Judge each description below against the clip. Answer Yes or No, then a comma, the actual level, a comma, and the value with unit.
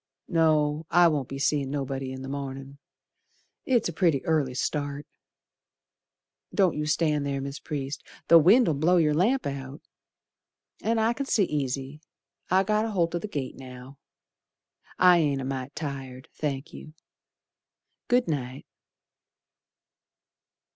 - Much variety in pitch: No, average, 4.0 semitones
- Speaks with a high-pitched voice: No, medium, 150 Hz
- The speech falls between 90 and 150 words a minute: Yes, slow, 135 wpm